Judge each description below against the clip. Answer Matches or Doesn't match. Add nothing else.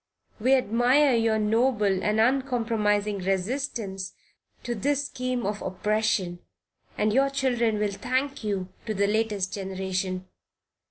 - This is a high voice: Matches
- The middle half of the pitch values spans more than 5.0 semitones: Doesn't match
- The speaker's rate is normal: Doesn't match